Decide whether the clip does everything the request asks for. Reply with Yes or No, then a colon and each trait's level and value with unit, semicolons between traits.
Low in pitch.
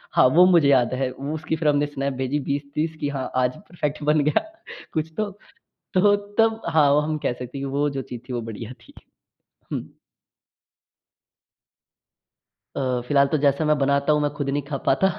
No: medium, 145 Hz